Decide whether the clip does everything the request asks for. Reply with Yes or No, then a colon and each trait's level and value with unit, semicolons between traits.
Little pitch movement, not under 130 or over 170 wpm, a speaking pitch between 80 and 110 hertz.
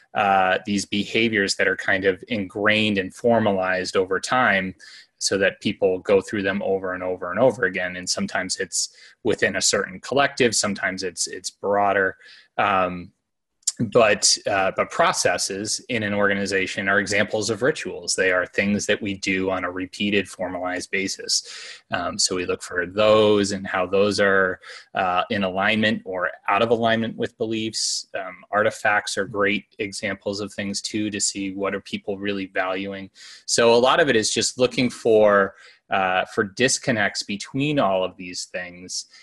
Yes: narrow, 2.1 semitones; average, 165 wpm; low, 100 Hz